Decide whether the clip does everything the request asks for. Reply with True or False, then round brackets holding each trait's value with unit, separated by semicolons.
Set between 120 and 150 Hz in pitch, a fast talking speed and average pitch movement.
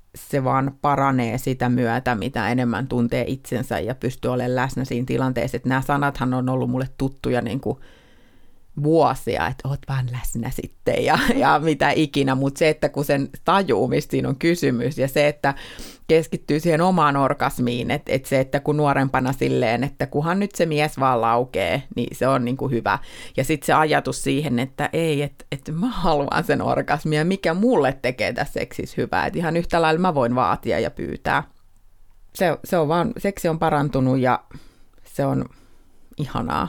True (135 Hz; 175 wpm; 3.3 semitones)